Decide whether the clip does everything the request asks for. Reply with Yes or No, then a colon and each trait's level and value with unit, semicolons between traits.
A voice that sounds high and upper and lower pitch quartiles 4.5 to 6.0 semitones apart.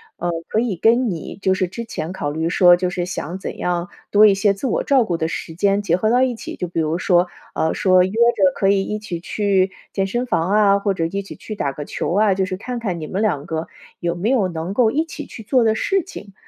No: high, 195 Hz; average, 3.8 semitones